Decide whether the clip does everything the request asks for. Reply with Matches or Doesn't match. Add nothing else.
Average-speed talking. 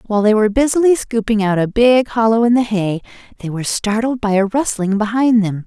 Doesn't match